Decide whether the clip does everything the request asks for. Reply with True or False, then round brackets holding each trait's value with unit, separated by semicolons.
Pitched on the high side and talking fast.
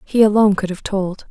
True (200 Hz; 230 wpm)